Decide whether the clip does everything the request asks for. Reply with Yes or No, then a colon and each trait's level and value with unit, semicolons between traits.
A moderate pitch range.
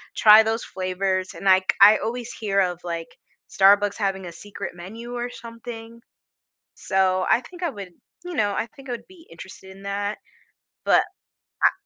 Yes: average, 3.4 semitones